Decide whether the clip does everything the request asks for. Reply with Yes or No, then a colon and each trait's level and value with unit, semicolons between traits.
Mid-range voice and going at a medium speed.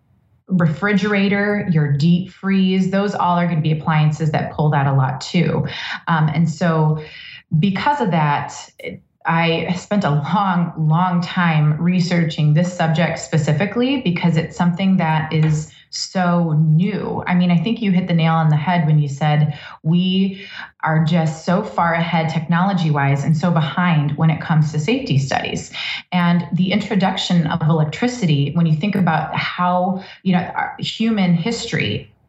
Yes: medium, 170 Hz; average, 160 wpm